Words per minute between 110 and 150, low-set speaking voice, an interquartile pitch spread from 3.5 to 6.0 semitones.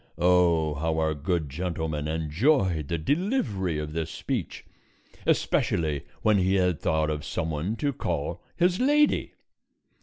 Yes: average, 140 wpm; very low, 85 Hz; average, 4.0 semitones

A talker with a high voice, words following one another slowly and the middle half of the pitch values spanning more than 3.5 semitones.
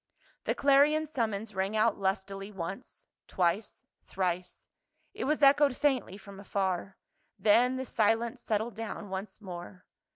Yes: high, 210 Hz; slow, 130 wpm; average, 4.3 semitones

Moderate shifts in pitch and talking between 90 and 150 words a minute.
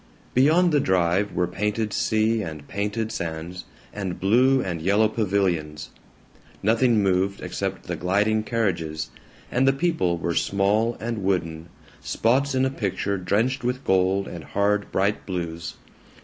Yes: average, 4.2 semitones; average, 140 wpm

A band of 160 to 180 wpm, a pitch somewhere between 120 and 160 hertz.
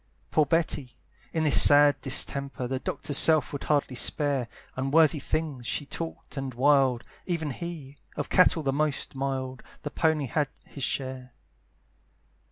No: average, 145 wpm; medium, 140 Hz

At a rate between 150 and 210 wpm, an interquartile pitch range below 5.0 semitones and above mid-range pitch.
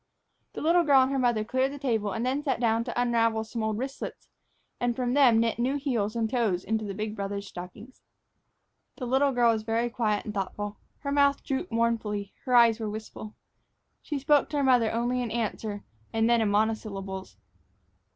Yes: average, 195 wpm; average, 3.2 semitones; high, 230 Hz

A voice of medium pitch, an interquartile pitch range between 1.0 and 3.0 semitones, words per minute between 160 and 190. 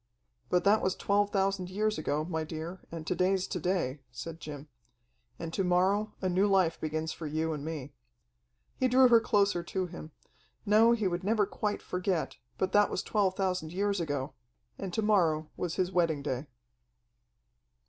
No: medium, 180 Hz; average, 4.0 semitones; average, 180 wpm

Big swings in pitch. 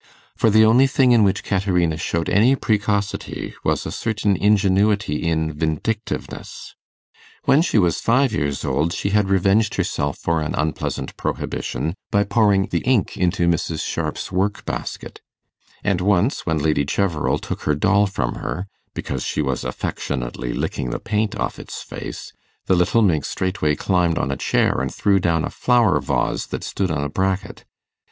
No: average, 4.6 semitones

